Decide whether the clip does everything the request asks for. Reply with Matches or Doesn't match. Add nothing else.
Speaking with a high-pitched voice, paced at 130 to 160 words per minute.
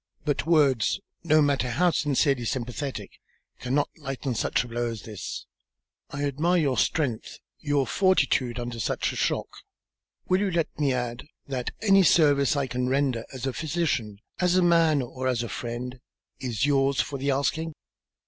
Doesn't match